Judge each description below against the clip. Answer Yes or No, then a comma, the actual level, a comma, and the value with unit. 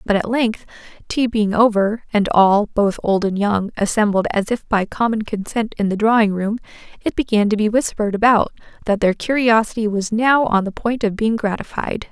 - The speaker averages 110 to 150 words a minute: No, average, 195 wpm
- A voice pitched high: Yes, high, 215 Hz